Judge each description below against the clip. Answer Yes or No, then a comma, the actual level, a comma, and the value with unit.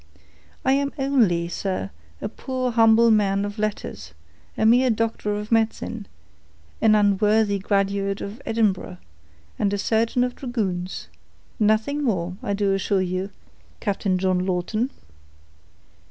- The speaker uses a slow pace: Yes, slow, 125 wpm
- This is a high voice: Yes, high, 210 Hz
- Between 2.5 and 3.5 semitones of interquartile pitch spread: Yes, average, 2.8 semitones